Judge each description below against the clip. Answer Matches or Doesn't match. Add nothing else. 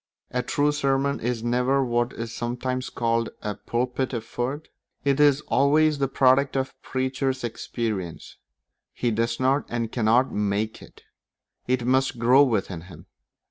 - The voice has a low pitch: Matches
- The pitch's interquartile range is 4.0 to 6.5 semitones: Doesn't match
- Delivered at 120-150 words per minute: Matches